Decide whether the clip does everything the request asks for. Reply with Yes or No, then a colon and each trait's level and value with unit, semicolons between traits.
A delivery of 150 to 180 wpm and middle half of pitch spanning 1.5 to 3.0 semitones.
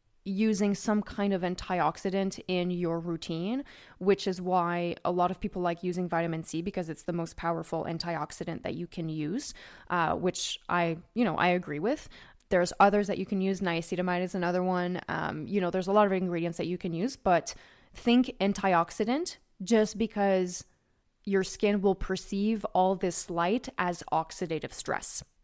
Yes: average, 175 wpm; average, 2.7 semitones